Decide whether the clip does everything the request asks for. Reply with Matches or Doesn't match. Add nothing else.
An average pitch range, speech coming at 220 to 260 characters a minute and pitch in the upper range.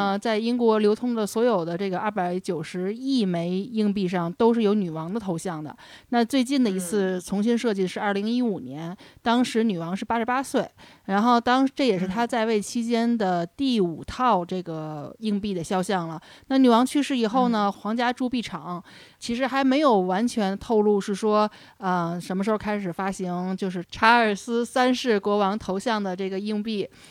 Doesn't match